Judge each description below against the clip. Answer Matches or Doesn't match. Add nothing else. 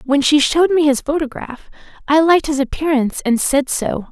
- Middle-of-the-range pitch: Doesn't match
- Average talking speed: Matches